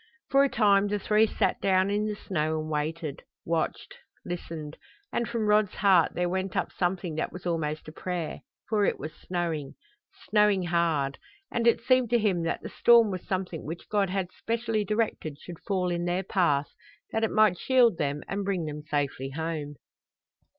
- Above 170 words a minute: Yes, average, 185 wpm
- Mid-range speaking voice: Yes, medium, 180 Hz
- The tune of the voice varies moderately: Yes, average, 4.7 semitones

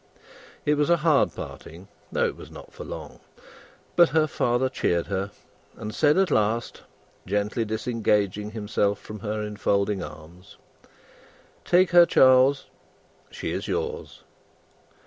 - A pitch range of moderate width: No, wide, 6.4 semitones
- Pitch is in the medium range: No, low, 110 Hz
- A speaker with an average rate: No, slow, 130 wpm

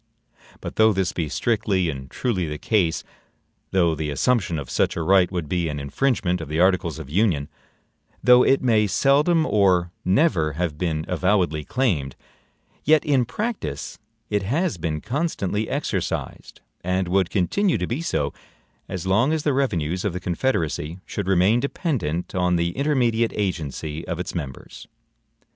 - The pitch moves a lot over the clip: Yes, wide, 6.5 semitones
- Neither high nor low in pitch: No, very low, 95 Hz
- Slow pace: No, average, 155 wpm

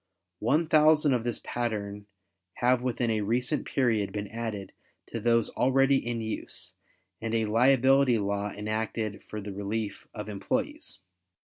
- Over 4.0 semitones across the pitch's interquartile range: No, average, 3.2 semitones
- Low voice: Yes, low, 115 Hz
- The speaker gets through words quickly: No, average, 140 wpm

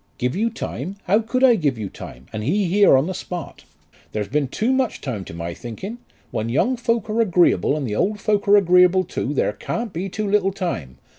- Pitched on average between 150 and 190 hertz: Yes, medium, 185 Hz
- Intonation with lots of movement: Yes, wide, 8.4 semitones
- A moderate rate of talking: No, fast, 220 wpm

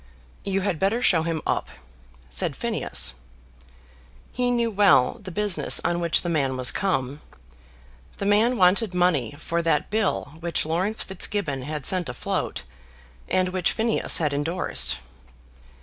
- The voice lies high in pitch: No, medium, 175 Hz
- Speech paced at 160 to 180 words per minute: No, average, 140 wpm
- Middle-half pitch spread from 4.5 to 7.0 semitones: Yes, average, 5.1 semitones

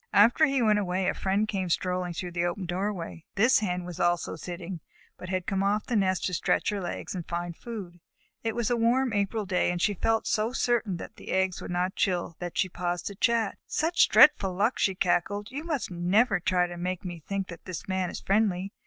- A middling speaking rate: No, fast, 225 wpm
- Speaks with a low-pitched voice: No, high, 190 Hz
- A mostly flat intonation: No, average, 3.2 semitones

